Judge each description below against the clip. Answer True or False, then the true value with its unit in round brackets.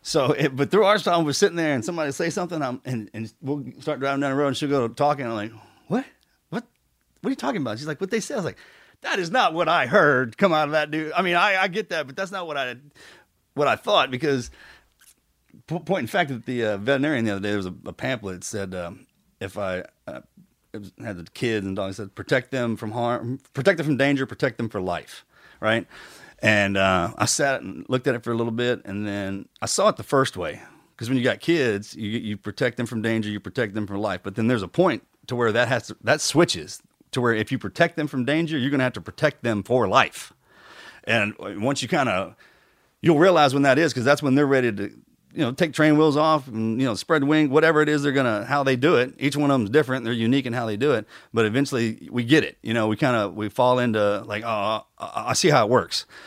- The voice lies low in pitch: True (130 Hz)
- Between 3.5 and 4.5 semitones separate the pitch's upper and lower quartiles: False (5.5 semitones)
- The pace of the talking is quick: True (265 wpm)